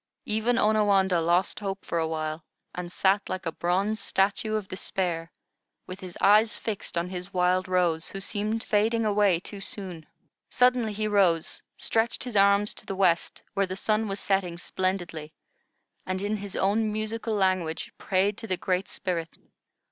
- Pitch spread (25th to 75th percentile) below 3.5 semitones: Yes, average, 2.9 semitones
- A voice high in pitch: Yes, high, 195 Hz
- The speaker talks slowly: No, average, 165 wpm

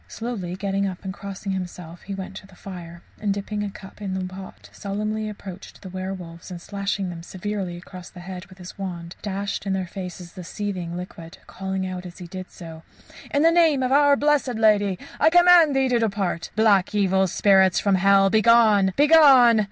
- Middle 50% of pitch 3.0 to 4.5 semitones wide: No, narrow, 2.6 semitones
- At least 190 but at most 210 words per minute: Yes, average, 195 wpm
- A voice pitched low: No, high, 195 Hz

